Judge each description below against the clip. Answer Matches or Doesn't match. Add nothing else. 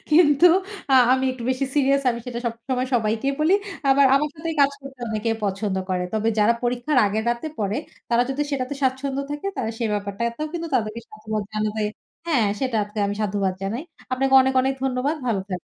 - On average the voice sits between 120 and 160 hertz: Doesn't match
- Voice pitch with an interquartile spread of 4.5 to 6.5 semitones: Doesn't match